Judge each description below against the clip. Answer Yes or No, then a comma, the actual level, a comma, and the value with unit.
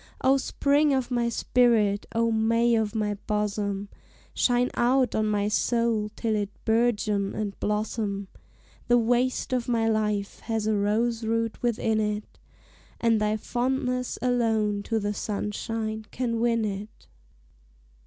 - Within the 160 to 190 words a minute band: No, slow, 135 wpm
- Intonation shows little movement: Yes, narrow, 2.3 semitones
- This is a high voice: Yes, high, 225 Hz